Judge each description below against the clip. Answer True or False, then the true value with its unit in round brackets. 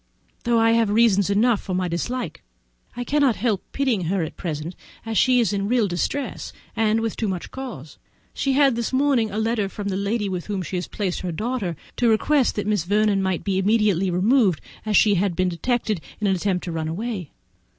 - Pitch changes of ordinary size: True (4.0 semitones)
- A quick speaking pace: True (210 wpm)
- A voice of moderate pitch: False (210 Hz)